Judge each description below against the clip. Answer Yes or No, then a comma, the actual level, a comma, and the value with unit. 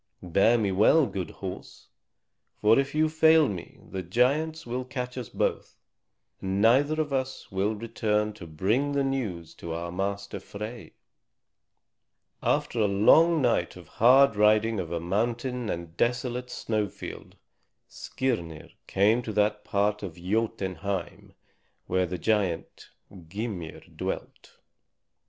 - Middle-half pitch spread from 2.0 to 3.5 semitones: No, average, 4.7 semitones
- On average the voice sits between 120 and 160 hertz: No, low, 105 Hz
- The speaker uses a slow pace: Yes, slow, 130 wpm